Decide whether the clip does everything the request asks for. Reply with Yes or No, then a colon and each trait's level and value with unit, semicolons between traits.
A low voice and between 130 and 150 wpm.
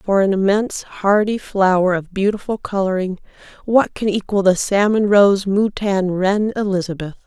No: high, 195 Hz; average, 140 wpm